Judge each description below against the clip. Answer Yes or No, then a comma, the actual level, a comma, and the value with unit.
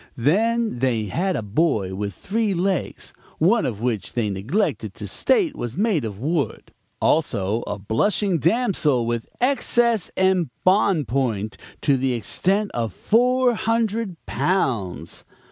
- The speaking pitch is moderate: Yes, medium, 160 Hz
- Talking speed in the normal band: No, slow, 130 wpm